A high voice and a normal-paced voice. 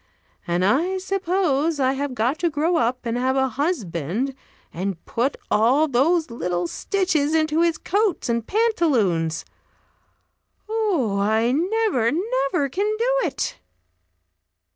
No: very high, 280 Hz; slow, 125 wpm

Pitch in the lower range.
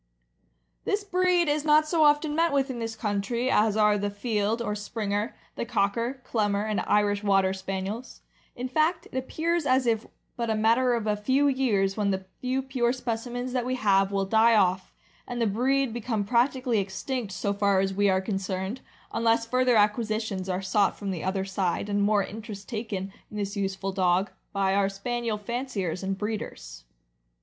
No: high, 215 Hz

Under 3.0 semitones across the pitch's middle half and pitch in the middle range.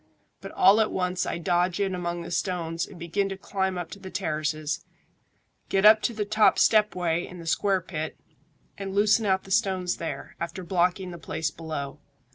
Yes: narrow, 2.6 semitones; medium, 180 Hz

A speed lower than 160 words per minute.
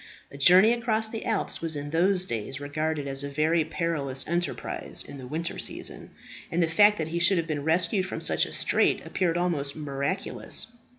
No: average, 190 wpm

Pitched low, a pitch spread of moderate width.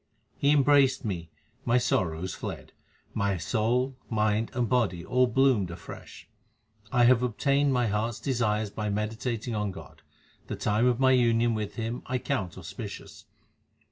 Yes: low, 115 Hz; average, 3.4 semitones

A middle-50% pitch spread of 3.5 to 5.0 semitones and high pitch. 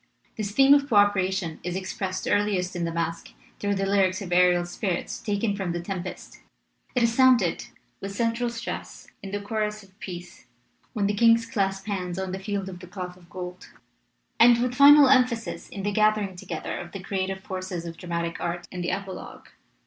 No: average, 2.9 semitones; high, 195 Hz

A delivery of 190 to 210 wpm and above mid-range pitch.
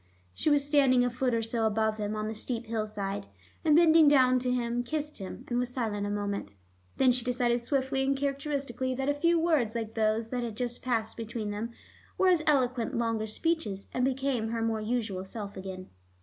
Yes: fast, 205 wpm; high, 240 Hz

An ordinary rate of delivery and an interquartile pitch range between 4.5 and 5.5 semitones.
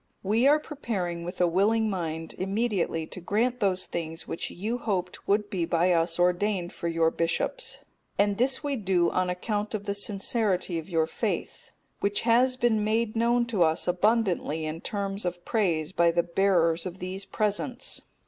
No: average, 175 wpm; average, 4.1 semitones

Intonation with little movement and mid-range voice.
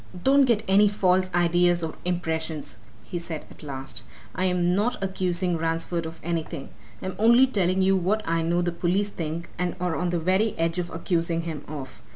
Yes: narrow, 2.3 semitones; medium, 175 Hz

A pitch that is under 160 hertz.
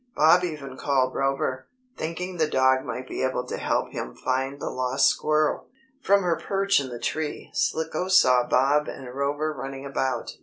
Yes: medium, 140 Hz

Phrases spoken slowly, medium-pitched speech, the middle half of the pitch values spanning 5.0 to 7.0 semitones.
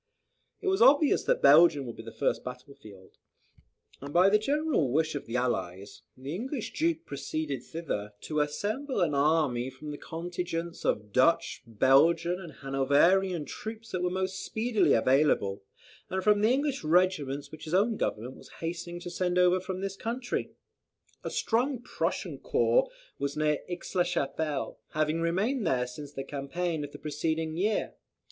No: average, 165 wpm; medium, 165 Hz; wide, 5.4 semitones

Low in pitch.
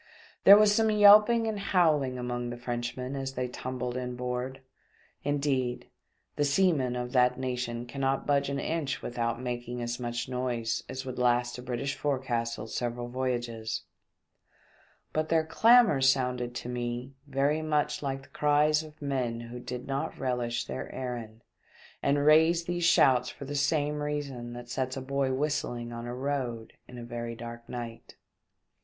Yes: low, 130 Hz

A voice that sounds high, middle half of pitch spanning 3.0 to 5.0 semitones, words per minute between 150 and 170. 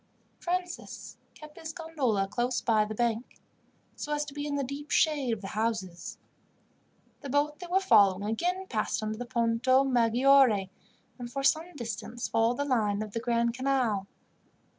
Yes: high, 245 Hz; average, 4.6 semitones; average, 165 wpm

